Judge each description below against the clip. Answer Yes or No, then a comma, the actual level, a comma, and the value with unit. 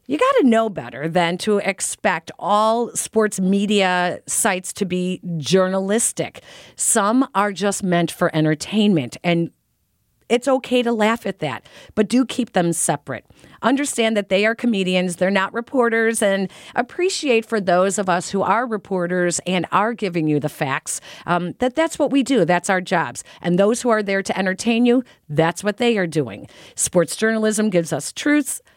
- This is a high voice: Yes, high, 195 Hz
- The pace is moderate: Yes, average, 170 wpm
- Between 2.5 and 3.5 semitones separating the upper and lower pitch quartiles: No, average, 4.6 semitones